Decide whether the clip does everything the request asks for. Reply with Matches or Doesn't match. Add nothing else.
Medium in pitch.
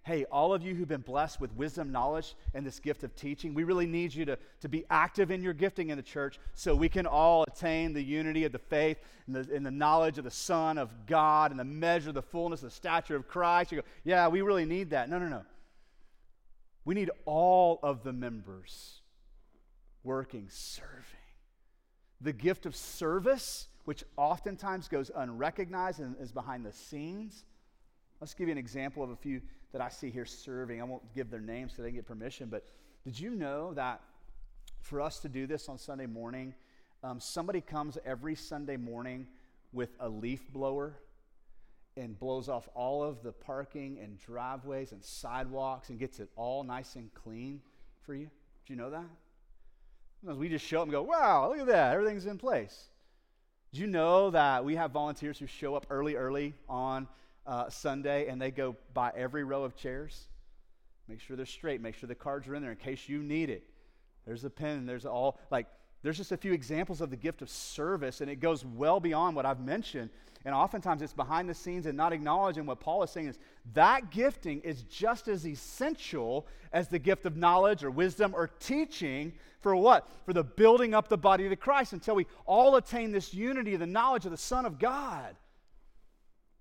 Matches